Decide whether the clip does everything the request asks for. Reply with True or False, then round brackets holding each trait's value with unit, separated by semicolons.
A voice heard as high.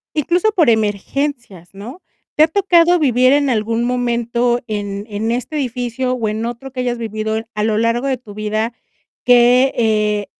True (240 Hz)